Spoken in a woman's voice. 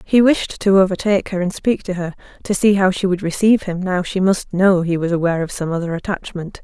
Yes: female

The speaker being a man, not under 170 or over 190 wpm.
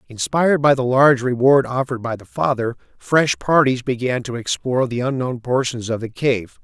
Yes: male; average, 180 wpm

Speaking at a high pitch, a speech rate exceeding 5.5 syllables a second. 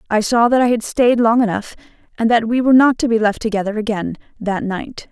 Yes: high, 225 Hz; 5.9 syllables/s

